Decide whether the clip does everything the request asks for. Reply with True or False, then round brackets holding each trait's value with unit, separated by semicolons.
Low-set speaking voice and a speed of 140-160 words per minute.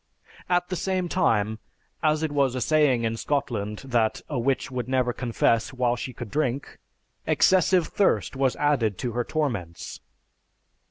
True (130 Hz; 155 wpm)